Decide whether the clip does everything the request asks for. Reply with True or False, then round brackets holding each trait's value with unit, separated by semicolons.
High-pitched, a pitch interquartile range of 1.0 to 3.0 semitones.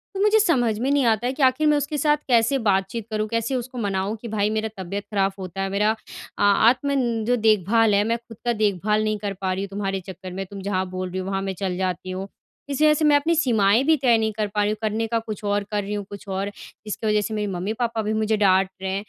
False (215 Hz; 3.4 semitones)